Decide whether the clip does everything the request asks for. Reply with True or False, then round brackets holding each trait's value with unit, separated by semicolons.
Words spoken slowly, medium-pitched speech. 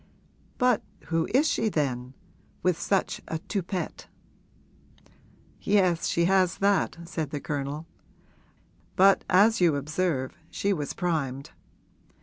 True (115 wpm; 170 Hz)